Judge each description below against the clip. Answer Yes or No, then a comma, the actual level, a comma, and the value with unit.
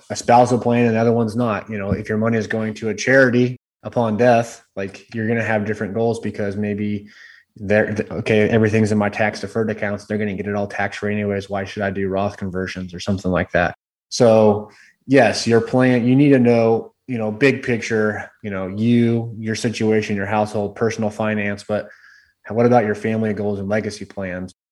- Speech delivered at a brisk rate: Yes, fast, 210 wpm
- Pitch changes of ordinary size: No, narrow, 2.1 semitones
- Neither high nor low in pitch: No, low, 105 Hz